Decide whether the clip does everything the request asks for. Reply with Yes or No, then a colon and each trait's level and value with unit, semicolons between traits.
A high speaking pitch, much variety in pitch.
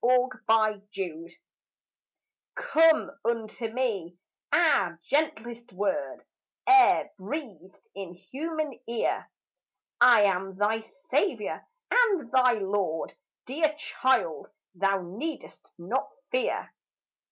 Yes: high, 230 Hz; wide, 7.0 semitones